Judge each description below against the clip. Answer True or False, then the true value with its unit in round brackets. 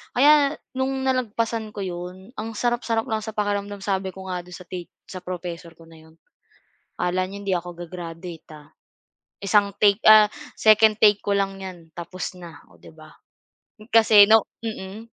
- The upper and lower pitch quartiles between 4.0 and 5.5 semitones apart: False (3.6 semitones)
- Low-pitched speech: False (195 Hz)